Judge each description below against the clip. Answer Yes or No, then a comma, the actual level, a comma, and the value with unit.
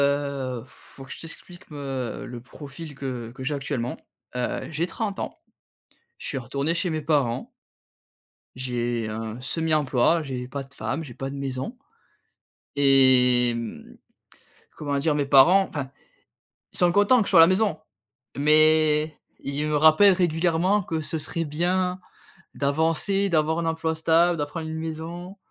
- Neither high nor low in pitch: Yes, medium, 150 Hz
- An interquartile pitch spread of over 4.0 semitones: No, average, 3.6 semitones